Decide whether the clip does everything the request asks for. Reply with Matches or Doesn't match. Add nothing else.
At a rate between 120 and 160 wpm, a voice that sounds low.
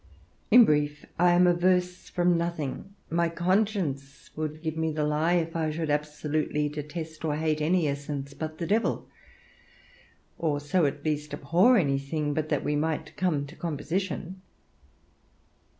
Doesn't match